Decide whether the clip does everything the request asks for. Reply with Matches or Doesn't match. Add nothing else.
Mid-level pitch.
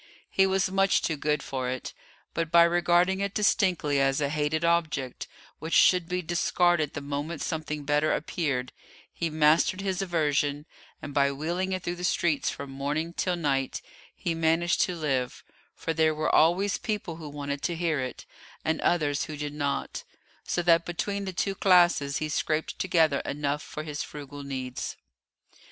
Matches